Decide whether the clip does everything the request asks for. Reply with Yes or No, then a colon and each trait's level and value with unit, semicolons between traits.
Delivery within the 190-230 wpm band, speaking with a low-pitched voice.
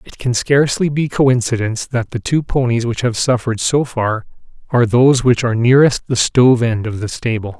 Yes: average, 200 wpm; low, 120 Hz